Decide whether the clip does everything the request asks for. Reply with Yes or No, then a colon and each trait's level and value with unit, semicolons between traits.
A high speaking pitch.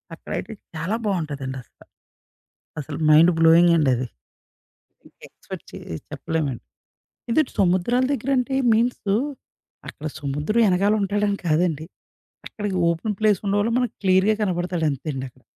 No: medium, 180 Hz